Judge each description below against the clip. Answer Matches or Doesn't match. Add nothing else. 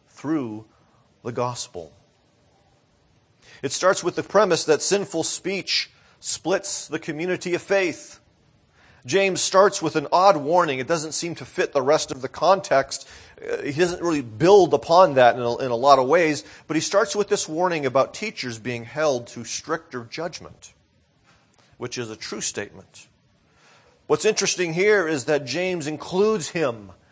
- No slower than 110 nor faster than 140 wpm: Doesn't match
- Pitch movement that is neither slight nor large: Doesn't match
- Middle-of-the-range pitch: Matches